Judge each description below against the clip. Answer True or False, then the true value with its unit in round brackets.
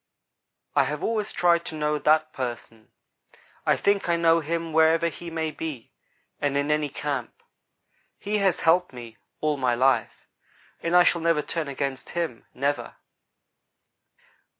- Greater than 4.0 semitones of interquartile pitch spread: False (3.3 semitones)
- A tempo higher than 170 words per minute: False (150 wpm)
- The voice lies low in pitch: False (155 Hz)